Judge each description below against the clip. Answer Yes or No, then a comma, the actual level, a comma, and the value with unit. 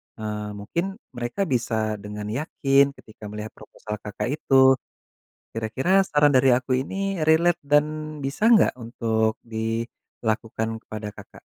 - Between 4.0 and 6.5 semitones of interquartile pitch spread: Yes, average, 5.2 semitones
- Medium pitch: No, low, 120 Hz